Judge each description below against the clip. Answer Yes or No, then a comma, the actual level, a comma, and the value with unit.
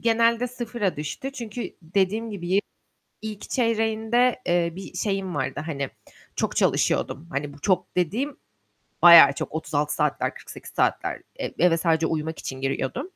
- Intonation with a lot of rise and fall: Yes, wide, 6.1 semitones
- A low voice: No, high, 190 Hz